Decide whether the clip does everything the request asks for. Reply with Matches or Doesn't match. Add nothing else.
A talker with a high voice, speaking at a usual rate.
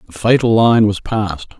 Doesn't match